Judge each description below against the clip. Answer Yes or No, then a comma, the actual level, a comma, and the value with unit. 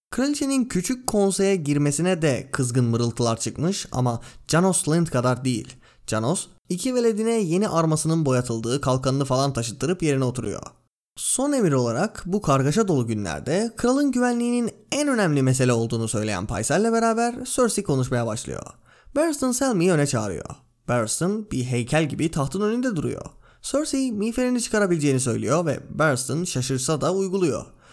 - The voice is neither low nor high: Yes, medium, 155 Hz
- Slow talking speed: No, average, 135 wpm